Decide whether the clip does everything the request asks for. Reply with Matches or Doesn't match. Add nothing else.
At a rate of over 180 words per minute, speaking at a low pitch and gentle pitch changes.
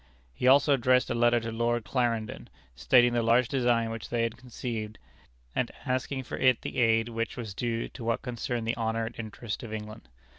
Matches